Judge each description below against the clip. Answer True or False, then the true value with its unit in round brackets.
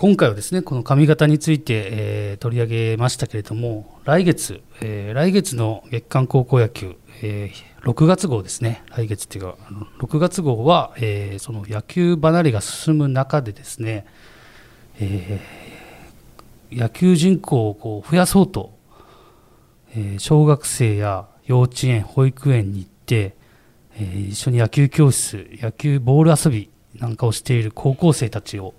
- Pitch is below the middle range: True (115 Hz)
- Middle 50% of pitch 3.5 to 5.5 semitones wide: True (5.2 semitones)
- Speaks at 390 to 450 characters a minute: False (280 characters per minute)